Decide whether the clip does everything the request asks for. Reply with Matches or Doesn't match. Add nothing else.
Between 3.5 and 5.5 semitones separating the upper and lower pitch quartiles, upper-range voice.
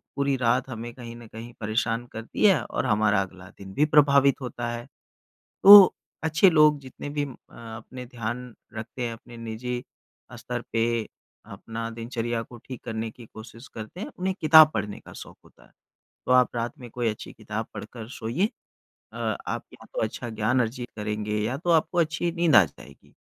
Doesn't match